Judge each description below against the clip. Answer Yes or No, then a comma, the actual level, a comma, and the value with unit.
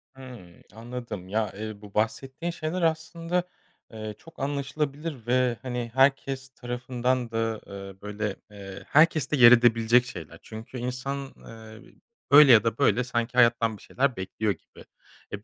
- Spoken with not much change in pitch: No, average, 3.6 semitones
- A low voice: Yes, low, 120 Hz